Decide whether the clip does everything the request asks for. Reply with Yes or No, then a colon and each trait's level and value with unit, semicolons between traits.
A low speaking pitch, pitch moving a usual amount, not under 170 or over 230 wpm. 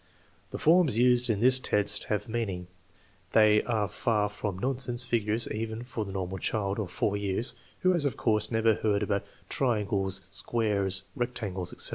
Yes: low, 110 Hz; average, 3.2 semitones; average, 180 wpm